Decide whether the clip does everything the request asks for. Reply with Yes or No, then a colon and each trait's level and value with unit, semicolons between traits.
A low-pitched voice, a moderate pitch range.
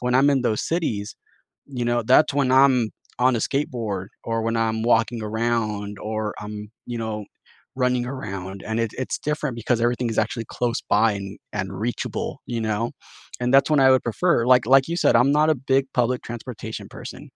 Yes: low, 120 Hz; average, 3.0 semitones